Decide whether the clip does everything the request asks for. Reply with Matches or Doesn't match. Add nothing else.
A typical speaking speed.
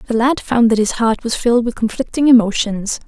Doesn't match